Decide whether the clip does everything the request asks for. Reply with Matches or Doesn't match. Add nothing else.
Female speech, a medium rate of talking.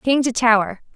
Matches